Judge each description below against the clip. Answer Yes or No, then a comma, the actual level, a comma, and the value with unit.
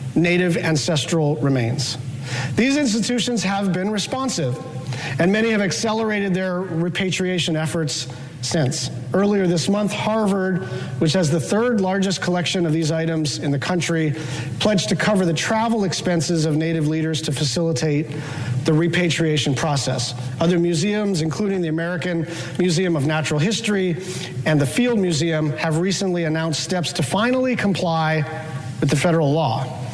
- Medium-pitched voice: Yes, medium, 165 Hz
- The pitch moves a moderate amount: Yes, average, 3.7 semitones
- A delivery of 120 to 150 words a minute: Yes, average, 140 wpm